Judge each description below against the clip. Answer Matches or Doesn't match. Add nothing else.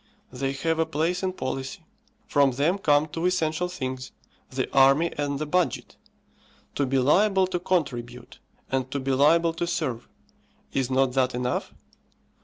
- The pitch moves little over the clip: Doesn't match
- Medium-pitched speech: Matches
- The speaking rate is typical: Matches